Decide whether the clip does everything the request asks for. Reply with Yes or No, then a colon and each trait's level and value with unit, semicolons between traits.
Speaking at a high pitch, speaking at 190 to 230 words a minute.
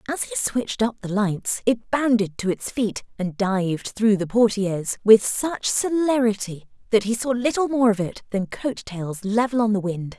Yes: high, 220 Hz; average, 195 wpm